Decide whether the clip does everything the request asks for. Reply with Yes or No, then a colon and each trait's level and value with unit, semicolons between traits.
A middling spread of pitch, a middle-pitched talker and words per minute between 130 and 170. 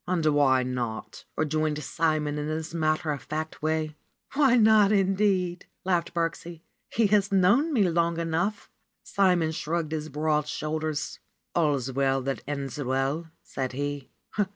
Yes: average, 3.4 semitones; medium, 155 Hz; average, 150 wpm